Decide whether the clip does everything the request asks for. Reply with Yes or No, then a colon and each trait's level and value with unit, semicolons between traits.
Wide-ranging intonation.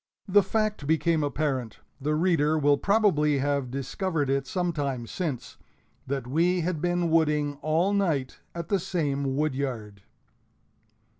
No: average, 4.2 semitones